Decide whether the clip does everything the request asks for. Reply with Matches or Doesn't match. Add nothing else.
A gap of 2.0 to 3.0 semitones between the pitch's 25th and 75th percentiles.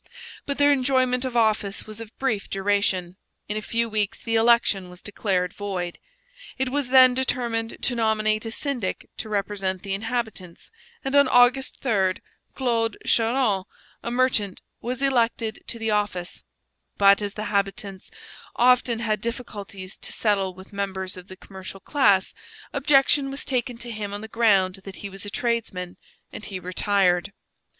Doesn't match